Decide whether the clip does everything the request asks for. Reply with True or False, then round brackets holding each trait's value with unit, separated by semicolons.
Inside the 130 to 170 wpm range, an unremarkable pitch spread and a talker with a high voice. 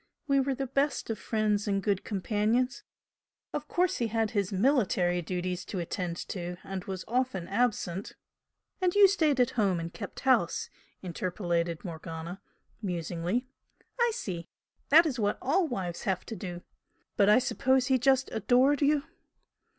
False (160 wpm; 6.3 semitones; 210 Hz)